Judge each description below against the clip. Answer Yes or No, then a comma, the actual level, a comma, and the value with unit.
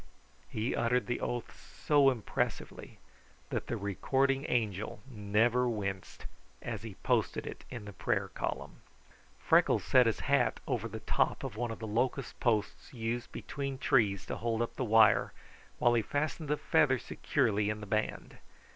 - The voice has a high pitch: No, low, 120 Hz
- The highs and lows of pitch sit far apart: No, average, 3.3 semitones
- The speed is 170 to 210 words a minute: No, average, 160 wpm